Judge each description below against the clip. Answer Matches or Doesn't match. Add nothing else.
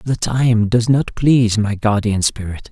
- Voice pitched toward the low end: Matches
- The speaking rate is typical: Matches